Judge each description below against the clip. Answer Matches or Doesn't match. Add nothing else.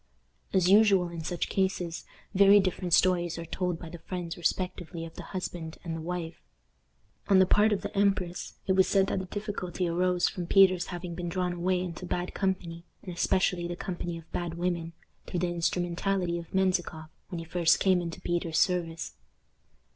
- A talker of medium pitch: Matches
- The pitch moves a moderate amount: Doesn't match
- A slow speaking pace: Doesn't match